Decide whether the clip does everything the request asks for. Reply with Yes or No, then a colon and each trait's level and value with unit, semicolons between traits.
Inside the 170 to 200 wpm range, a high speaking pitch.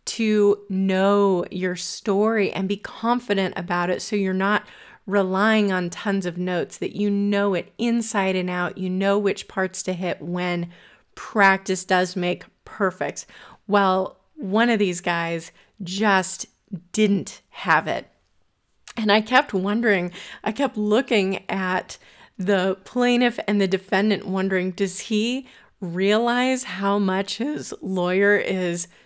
No: slow, 135 wpm; high, 195 Hz